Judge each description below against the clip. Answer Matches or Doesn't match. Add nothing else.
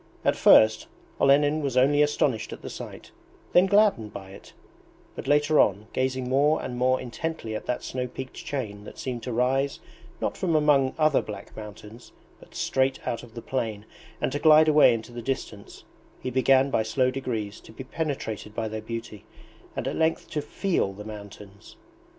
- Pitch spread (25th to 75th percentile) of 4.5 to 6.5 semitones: Matches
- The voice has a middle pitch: Doesn't match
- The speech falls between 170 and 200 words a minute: Matches